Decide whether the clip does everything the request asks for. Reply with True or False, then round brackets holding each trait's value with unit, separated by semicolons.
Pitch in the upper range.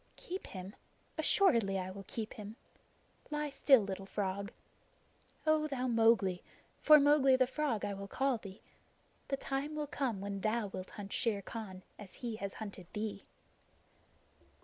True (220 Hz)